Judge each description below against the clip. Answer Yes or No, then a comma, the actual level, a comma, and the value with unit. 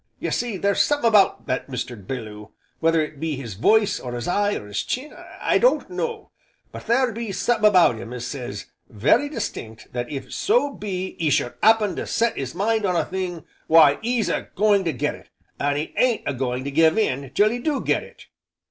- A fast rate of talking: Yes, fast, 210 wpm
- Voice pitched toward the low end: No, medium, 175 Hz